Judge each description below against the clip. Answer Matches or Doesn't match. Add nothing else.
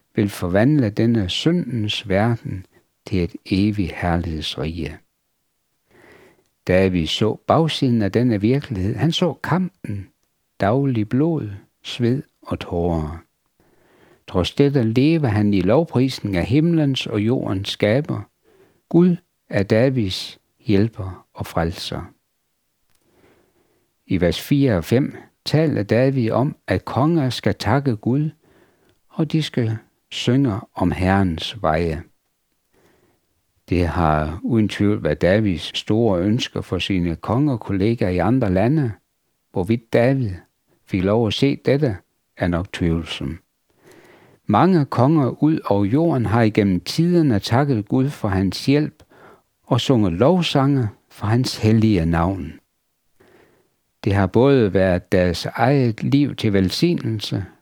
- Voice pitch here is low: Matches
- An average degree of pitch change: Doesn't match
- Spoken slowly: Matches